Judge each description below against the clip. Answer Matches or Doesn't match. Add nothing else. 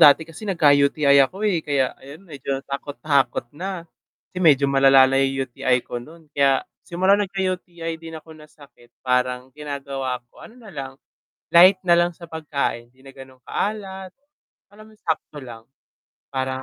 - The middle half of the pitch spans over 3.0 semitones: Matches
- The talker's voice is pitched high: Doesn't match